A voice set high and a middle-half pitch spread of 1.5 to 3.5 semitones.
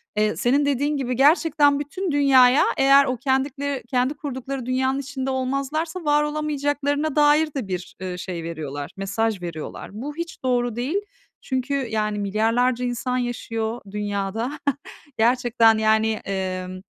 No: very high, 255 Hz; average, 4.5 semitones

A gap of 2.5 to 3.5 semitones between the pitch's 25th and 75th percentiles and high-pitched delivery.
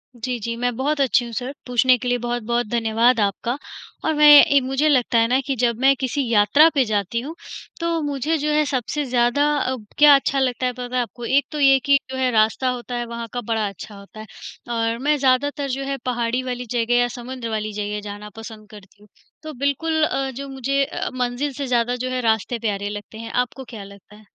Yes: average, 3.1 semitones; high, 245 Hz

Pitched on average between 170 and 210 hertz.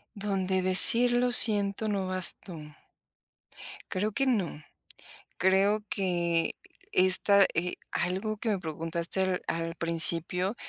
Yes: high, 190 Hz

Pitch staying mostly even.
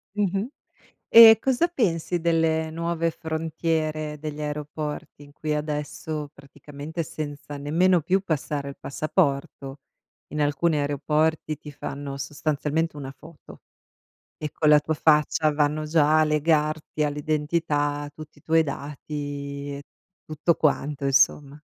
Yes: narrow, 1.7 semitones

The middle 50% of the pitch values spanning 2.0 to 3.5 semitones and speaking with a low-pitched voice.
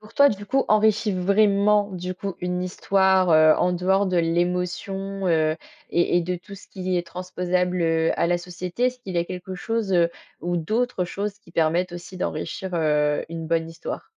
No: narrow, 2.4 semitones; medium, 180 Hz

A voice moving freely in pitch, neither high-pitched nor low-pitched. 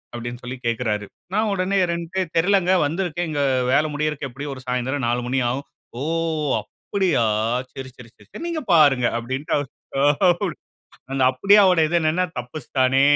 Yes: wide, 5.8 semitones; medium, 145 Hz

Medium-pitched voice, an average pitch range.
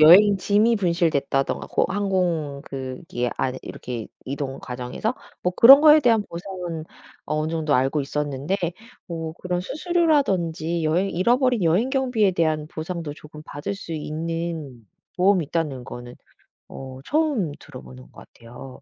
No: medium, 165 Hz; wide, 5.8 semitones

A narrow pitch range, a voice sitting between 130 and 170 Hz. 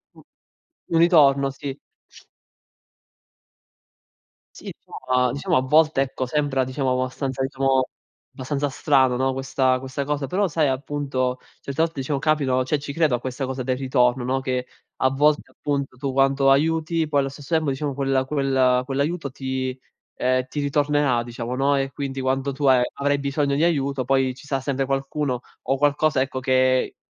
Yes: narrow, 1.7 semitones; low, 135 Hz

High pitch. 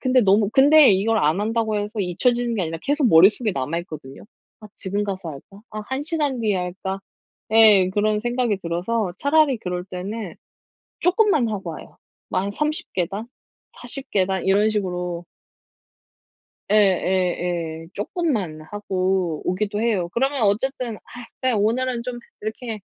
Yes: high, 210 Hz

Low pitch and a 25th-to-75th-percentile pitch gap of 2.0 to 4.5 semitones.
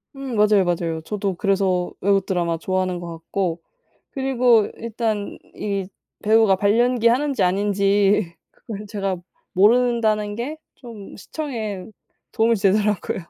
No: high, 205 Hz; average, 3.4 semitones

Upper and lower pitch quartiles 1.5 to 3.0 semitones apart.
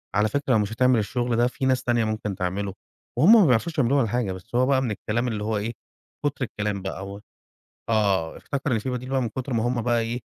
No: average, 3.4 semitones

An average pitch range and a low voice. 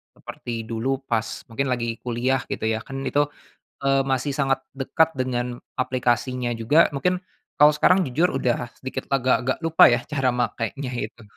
No: narrow, 2.2 semitones; low, 130 Hz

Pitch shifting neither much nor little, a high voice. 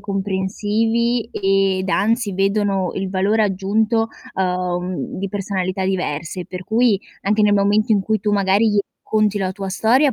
No: narrow, 2.2 semitones; high, 200 Hz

